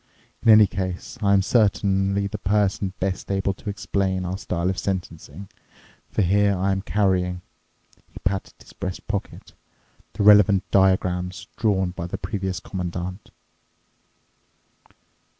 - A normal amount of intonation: No, narrow, 1.6 semitones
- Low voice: Yes, very low, 95 Hz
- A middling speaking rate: No, slow, 125 wpm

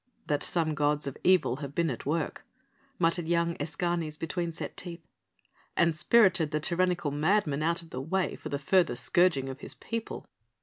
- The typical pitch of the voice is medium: Yes, medium, 165 Hz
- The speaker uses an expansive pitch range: No, average, 2.9 semitones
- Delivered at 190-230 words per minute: No, average, 175 wpm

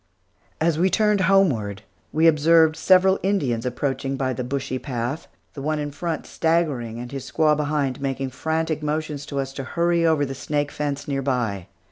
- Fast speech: No, average, 175 wpm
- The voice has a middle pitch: Yes, medium, 145 Hz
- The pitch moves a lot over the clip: No, average, 3.4 semitones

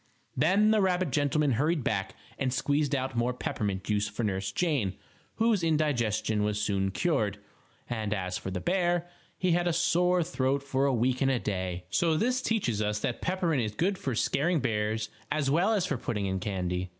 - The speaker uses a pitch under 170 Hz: Yes, low, 135 Hz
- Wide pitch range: Yes, wide, 8.4 semitones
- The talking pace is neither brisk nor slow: Yes, average, 190 wpm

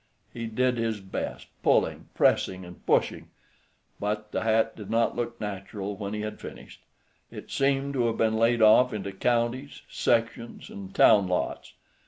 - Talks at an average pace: Yes, average, 160 wpm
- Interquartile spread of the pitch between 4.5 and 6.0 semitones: No, narrow, 2.5 semitones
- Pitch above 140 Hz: No, low, 110 Hz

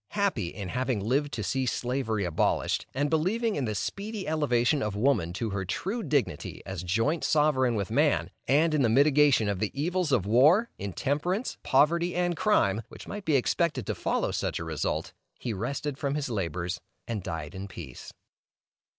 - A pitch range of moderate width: No, wide, 7.2 semitones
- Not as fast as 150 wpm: No, average, 175 wpm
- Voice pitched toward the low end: Yes, low, 130 Hz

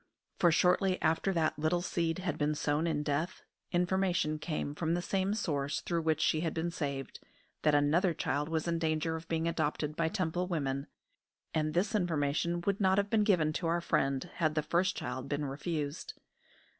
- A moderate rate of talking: Yes, average, 185 wpm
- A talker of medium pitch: Yes, medium, 165 Hz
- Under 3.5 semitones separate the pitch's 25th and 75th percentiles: Yes, average, 2.8 semitones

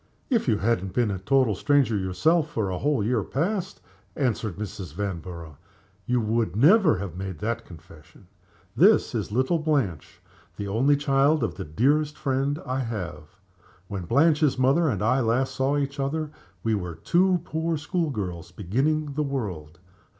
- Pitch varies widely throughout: Yes, wide, 7.0 semitones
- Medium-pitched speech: No, low, 120 Hz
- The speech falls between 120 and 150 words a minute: No, average, 165 wpm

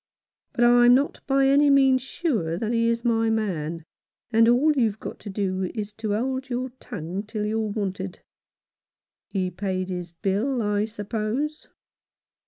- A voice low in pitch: No, high, 220 Hz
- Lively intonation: No, average, 4.1 semitones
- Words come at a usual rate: Yes, average, 155 wpm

